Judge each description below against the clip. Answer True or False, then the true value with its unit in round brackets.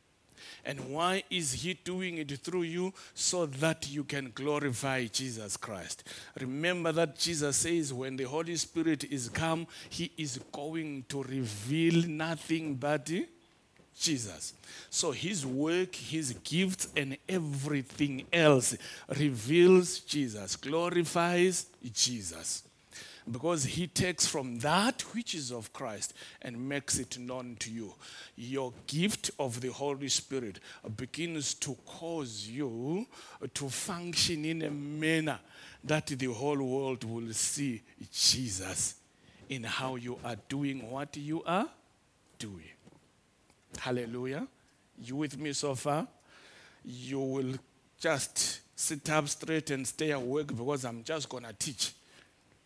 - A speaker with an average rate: False (130 wpm)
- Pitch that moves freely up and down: False (4.1 semitones)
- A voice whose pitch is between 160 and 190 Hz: False (145 Hz)